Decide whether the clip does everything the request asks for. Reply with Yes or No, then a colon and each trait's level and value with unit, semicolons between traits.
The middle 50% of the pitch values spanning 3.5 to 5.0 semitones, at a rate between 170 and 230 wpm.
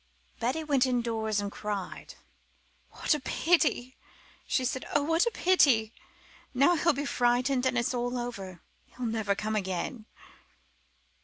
No: average, 4.3 semitones; average, 140 wpm